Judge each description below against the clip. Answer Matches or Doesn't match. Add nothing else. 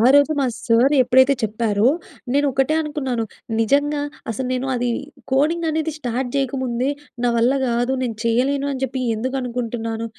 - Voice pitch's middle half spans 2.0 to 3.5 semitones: Matches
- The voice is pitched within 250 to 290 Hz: Matches